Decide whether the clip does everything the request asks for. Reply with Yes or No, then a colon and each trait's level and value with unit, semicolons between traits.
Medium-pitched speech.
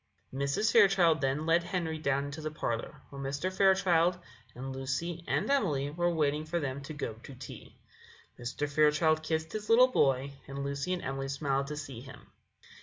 Yes: medium, 150 Hz